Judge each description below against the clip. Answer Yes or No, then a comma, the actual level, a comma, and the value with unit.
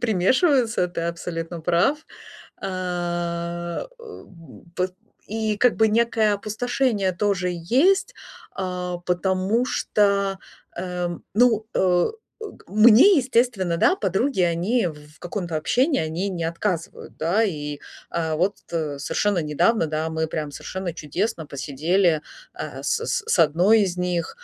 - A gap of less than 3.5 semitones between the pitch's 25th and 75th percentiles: No, average, 4.6 semitones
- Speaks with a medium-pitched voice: Yes, medium, 180 Hz